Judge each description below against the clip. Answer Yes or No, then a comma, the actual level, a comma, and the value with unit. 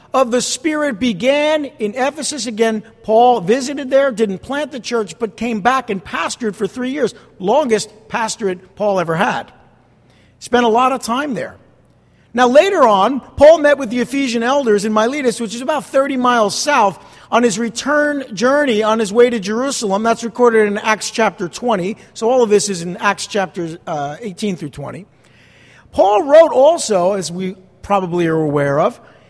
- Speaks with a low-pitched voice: No, high, 230 Hz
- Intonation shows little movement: No, average, 4.6 semitones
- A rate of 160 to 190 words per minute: Yes, average, 175 wpm